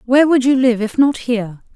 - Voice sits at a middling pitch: No, high, 245 Hz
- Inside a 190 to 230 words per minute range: No, fast, 240 wpm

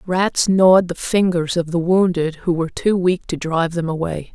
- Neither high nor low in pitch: Yes, medium, 175 Hz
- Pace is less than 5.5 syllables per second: Yes, 5.0 syllables/s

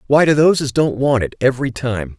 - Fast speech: Yes, fast, 245 wpm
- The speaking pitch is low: Yes, low, 130 Hz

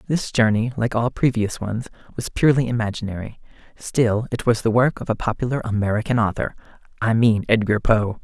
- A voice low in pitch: Yes, low, 115 Hz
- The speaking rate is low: No, average, 170 wpm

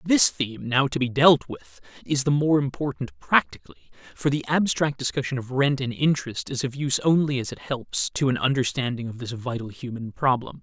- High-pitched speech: No, low, 135 Hz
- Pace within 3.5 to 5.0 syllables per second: No, 5.5 syllables/s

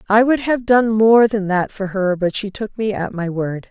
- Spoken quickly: Yes, fast, 260 wpm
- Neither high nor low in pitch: No, high, 205 Hz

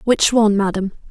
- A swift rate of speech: No, average, 165 wpm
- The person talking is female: Yes, female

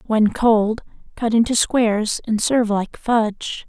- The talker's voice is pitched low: No, high, 220 Hz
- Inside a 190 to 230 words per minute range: No, average, 145 wpm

